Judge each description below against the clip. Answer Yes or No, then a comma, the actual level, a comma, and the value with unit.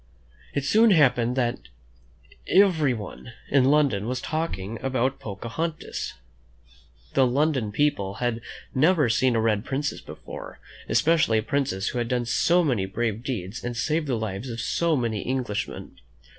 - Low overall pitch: Yes, low, 125 Hz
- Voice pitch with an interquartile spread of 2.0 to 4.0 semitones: No, average, 4.7 semitones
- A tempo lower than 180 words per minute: Yes, average, 145 wpm